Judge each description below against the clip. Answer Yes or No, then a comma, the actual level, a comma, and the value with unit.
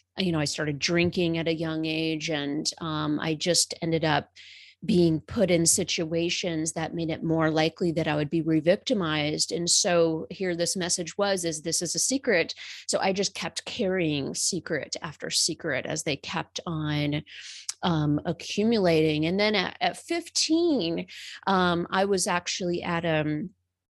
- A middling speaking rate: Yes, average, 165 wpm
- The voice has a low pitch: No, medium, 165 Hz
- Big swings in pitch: No, narrow, 2.6 semitones